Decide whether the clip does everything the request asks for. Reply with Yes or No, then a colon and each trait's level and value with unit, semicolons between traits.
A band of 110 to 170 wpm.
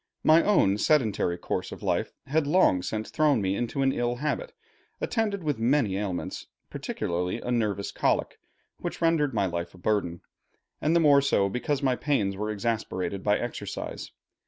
Yes: average, 165 wpm